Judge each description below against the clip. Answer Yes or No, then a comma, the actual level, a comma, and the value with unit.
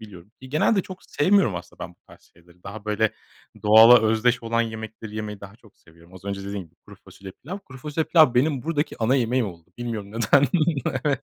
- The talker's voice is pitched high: No, low, 110 Hz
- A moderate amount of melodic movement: Yes, average, 4.6 semitones